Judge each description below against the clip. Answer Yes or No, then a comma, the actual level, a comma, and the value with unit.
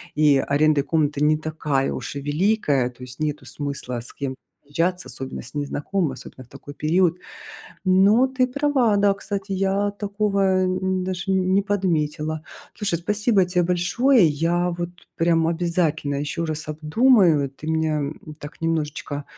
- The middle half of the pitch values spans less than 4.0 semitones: No, average, 4.6 semitones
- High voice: No, medium, 165 Hz